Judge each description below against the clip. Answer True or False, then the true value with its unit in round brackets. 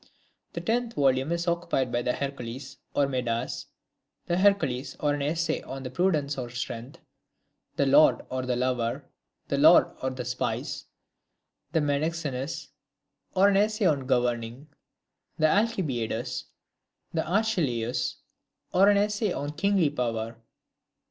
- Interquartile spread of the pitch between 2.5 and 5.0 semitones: False (5.5 semitones)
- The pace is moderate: False (130 wpm)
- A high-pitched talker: False (140 Hz)